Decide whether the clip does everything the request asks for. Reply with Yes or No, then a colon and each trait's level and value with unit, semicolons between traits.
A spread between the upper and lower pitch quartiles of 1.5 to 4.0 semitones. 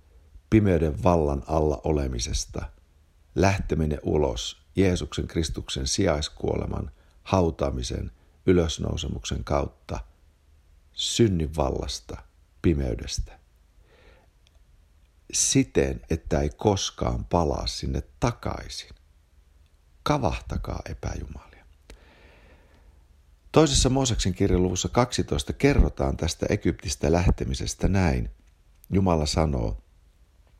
Yes: average, 3.7 semitones